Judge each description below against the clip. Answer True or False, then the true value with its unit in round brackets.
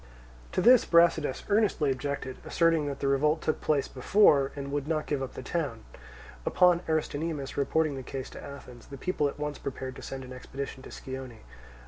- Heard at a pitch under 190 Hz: True (140 Hz)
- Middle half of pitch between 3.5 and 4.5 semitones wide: False (3.1 semitones)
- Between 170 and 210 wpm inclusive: True (185 wpm)